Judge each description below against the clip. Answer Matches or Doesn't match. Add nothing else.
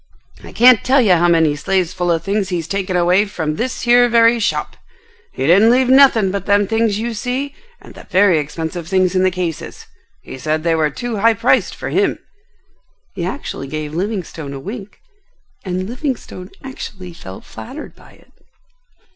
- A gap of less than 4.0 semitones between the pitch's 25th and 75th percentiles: Doesn't match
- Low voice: Doesn't match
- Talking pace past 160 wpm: Matches